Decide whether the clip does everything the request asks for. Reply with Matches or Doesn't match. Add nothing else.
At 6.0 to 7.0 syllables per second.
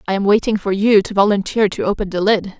Matches